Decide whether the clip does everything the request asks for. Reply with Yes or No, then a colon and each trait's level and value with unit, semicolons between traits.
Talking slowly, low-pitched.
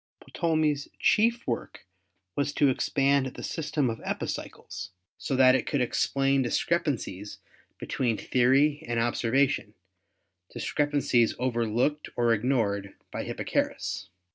Yes: slow, 115 wpm; low, 130 Hz